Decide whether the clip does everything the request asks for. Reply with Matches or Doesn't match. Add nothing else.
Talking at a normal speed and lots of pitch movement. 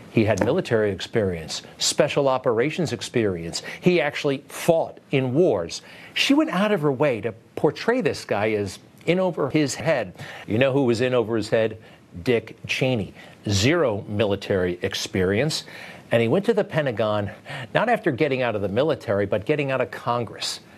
Matches